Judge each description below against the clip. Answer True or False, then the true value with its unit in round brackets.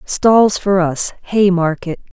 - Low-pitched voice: False (185 Hz)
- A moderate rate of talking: False (110 wpm)